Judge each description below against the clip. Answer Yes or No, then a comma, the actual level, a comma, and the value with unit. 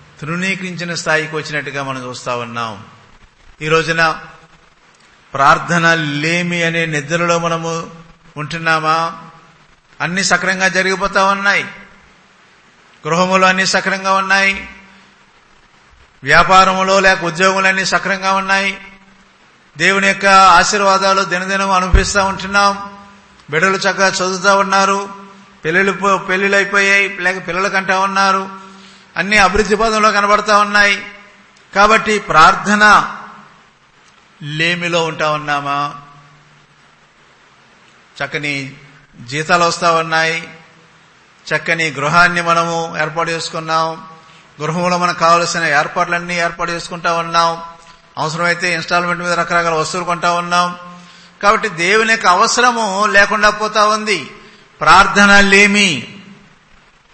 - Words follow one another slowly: Yes, slow, 90 wpm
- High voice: No, medium, 175 Hz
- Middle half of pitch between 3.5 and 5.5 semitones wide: No, average, 3.1 semitones